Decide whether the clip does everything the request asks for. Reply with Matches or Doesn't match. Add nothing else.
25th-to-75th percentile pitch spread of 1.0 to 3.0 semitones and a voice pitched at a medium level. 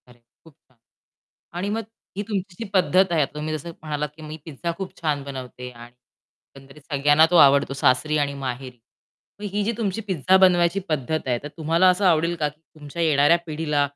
Doesn't match